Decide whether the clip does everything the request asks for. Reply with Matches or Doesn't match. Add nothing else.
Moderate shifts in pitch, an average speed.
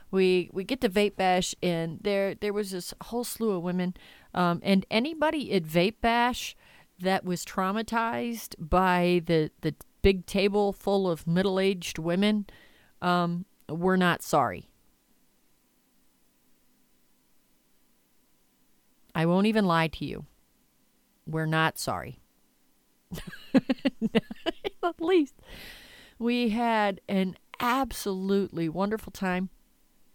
Doesn't match